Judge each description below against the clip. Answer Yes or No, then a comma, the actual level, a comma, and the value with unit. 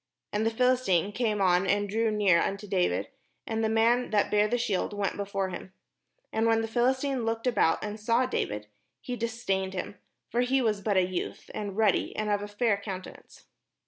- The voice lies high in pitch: Yes, high, 210 Hz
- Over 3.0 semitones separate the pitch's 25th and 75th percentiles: No, average, 2.7 semitones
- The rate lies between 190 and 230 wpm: Yes, average, 200 wpm